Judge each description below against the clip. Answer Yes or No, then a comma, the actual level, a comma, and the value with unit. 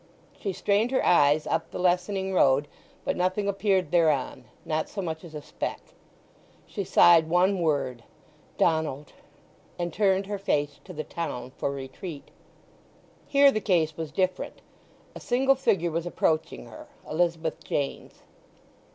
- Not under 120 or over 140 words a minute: Yes, slow, 135 wpm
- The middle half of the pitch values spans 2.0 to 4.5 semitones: Yes, average, 4.0 semitones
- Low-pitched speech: No, medium, 175 Hz